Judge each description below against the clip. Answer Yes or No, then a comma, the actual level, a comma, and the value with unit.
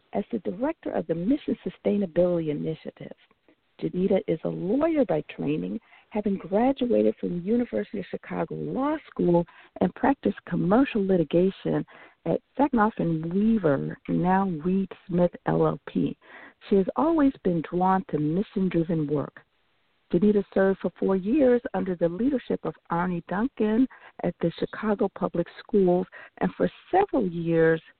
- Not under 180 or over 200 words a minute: No, slow, 135 wpm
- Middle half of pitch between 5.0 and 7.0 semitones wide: Yes, wide, 5.6 semitones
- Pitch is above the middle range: Yes, high, 195 Hz